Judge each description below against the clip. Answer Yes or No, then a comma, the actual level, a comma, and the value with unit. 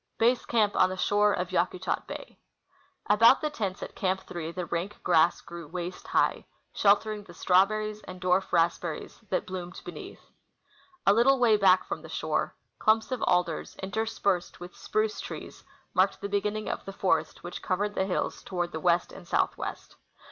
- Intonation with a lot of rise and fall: No, average, 2.9 semitones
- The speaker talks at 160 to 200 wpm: Yes, average, 175 wpm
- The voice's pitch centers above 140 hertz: Yes, high, 190 Hz